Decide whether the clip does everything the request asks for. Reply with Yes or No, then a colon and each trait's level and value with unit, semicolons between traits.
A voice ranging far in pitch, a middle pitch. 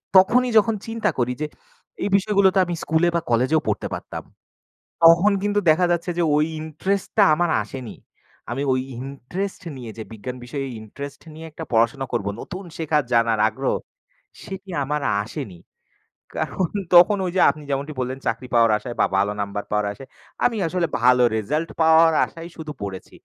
Yes: wide, 6.2 semitones; medium, 150 Hz